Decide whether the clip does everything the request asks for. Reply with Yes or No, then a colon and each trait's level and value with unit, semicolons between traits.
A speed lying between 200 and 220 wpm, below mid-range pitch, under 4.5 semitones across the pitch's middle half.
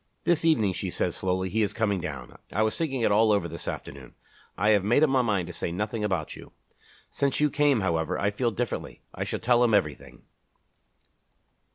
No: fast, 205 wpm; low, 105 Hz; average, 4.9 semitones